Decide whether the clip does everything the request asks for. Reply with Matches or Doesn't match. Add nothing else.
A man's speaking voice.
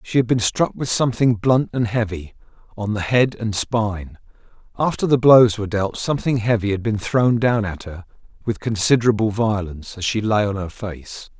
Matches